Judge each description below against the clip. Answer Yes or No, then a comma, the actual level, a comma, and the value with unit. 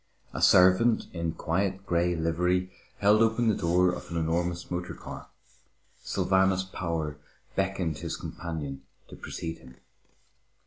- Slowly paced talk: Yes, slow, 130 wpm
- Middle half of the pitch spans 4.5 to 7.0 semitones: No, narrow, 2.4 semitones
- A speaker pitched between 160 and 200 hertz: No, very low, 90 Hz